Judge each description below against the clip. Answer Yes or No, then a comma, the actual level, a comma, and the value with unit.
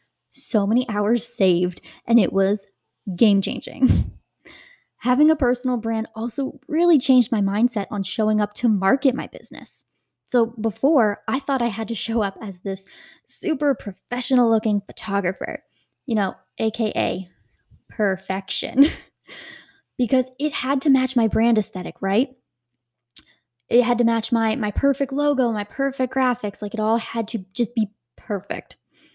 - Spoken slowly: No, average, 150 wpm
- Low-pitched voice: No, high, 225 Hz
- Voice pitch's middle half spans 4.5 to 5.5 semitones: No, average, 3.9 semitones